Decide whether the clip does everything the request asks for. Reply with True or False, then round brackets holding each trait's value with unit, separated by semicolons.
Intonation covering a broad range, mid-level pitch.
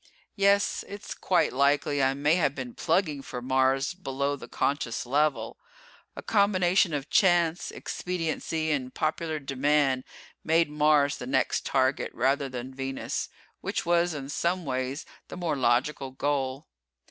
False (3.7 semitones; 145 Hz)